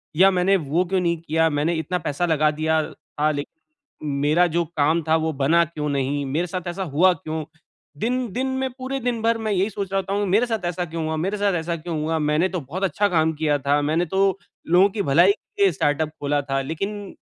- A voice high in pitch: No, medium, 170 Hz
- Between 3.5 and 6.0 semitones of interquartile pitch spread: Yes, average, 4.1 semitones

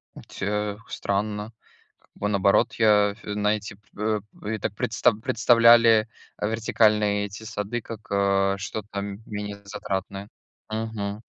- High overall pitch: No, low, 105 Hz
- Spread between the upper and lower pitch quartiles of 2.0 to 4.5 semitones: No, narrow, 1.4 semitones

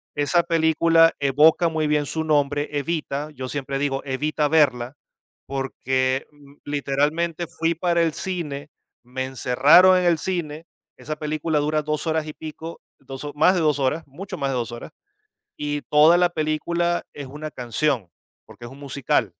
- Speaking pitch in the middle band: Yes, medium, 150 Hz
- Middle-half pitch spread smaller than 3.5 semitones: Yes, average, 2.9 semitones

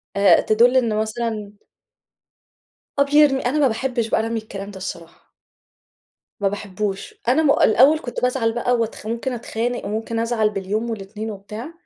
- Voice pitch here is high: Yes, high, 225 Hz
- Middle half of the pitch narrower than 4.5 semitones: Yes, average, 2.9 semitones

